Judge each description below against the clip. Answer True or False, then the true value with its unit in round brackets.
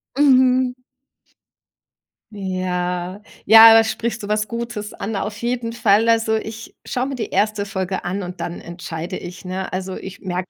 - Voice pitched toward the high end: True (210 Hz)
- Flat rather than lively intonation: False (3.6 semitones)